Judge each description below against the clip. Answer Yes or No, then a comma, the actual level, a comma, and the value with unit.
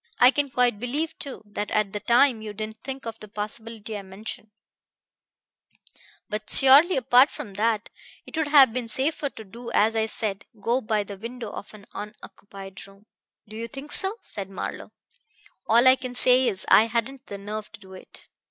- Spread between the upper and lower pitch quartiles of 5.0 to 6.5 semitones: No, average, 3.7 semitones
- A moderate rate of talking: Yes, average, 190 wpm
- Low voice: No, high, 225 Hz